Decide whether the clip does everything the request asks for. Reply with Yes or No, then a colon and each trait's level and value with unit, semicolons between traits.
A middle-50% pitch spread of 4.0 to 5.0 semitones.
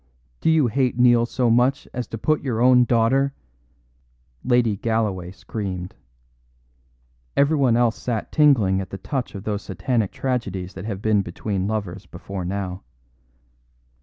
Yes: average, 4.5 semitones